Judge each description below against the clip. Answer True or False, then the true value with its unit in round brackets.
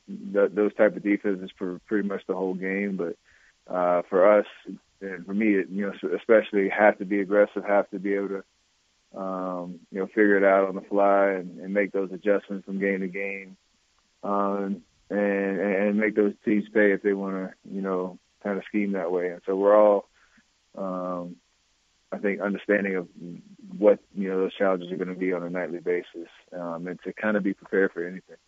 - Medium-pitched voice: False (95 Hz)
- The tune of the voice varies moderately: False (1.6 semitones)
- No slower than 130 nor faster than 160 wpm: False (205 wpm)